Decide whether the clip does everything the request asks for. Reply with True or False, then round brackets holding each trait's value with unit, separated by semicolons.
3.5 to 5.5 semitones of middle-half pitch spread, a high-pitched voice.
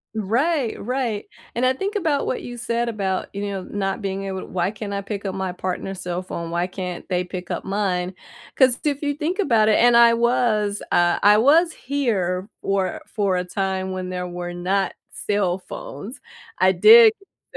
True (4.6 semitones; 200 Hz)